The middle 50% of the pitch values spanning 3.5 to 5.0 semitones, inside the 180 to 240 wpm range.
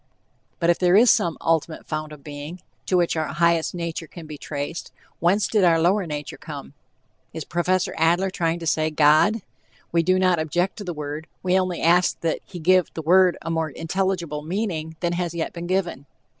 No: narrow, 2.5 semitones; average, 200 wpm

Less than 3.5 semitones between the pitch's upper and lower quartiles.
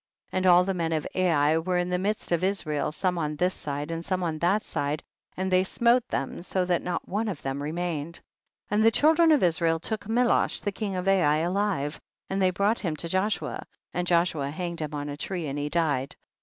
No: average, 3.8 semitones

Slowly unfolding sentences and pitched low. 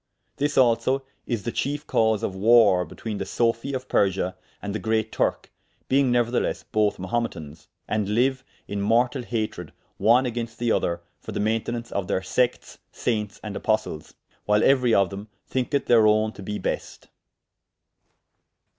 No: average, 155 wpm; low, 110 Hz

